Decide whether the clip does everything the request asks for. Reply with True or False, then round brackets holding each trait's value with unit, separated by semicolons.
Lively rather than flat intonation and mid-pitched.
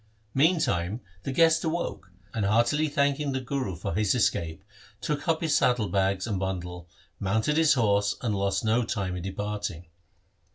False (6.5 semitones; 105 Hz)